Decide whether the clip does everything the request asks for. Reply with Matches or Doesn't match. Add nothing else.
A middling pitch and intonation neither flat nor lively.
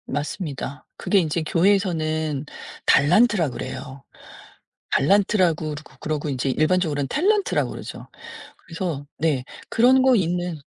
Matches